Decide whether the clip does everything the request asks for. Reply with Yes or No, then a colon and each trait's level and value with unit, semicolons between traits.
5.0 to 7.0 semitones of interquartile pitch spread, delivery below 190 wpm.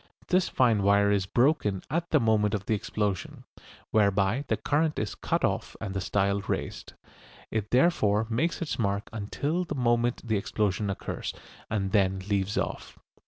No: average, 3.8 semitones; average, 165 wpm